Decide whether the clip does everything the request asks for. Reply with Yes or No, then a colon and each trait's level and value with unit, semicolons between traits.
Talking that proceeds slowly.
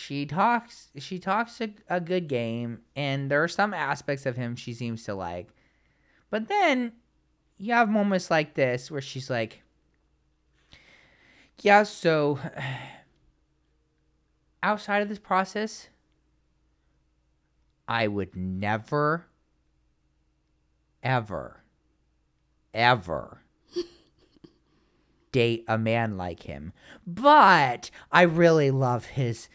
Yes: slow, 100 wpm